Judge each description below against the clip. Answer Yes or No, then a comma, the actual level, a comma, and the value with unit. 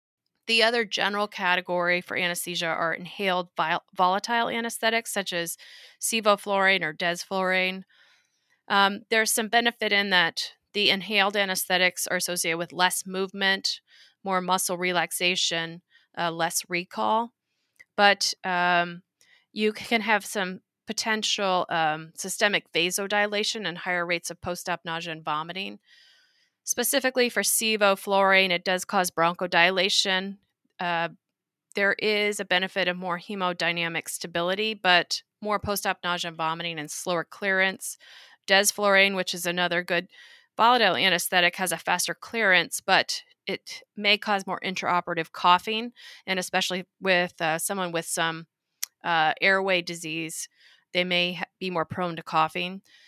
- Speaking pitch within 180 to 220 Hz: Yes, medium, 185 Hz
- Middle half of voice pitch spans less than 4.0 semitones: Yes, average, 2.8 semitones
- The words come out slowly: Yes, slow, 130 wpm